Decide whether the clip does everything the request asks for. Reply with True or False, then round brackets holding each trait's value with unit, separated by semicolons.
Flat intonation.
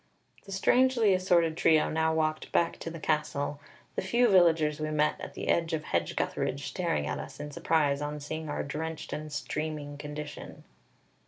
True (2.1 semitones)